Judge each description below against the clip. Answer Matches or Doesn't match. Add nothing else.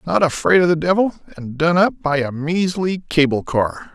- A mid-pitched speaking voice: Matches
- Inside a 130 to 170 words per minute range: Doesn't match